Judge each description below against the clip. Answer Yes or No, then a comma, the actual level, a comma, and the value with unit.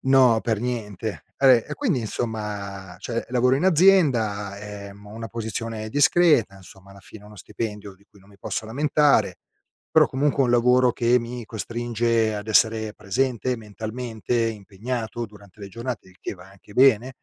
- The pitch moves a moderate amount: Yes, average, 3.2 semitones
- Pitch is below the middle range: Yes, low, 115 Hz